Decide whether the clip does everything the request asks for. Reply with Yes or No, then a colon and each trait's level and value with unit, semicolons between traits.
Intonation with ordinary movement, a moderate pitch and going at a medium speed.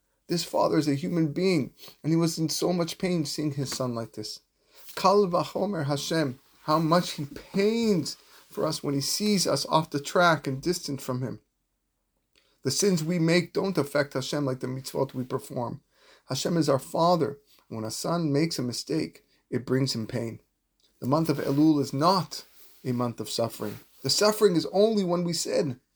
Yes: average, 4.7 semitones; medium, 150 Hz; average, 185 wpm